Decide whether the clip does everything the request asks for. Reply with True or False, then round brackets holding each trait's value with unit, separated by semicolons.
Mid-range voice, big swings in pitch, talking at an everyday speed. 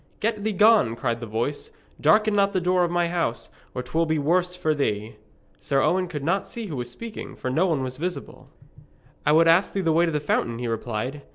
False (160 Hz; 6.2 semitones; 225 wpm)